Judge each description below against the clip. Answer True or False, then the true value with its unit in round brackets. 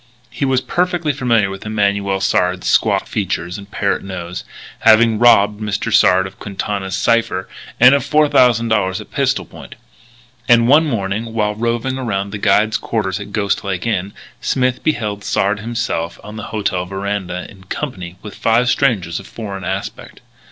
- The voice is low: True (105 Hz)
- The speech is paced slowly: False (160 wpm)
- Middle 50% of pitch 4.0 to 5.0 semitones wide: False (3.3 semitones)